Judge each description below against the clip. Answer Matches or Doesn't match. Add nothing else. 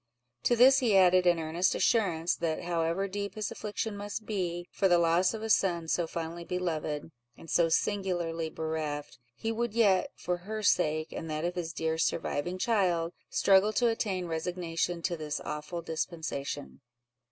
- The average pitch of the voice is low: Doesn't match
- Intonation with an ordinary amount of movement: Matches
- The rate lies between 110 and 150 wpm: Doesn't match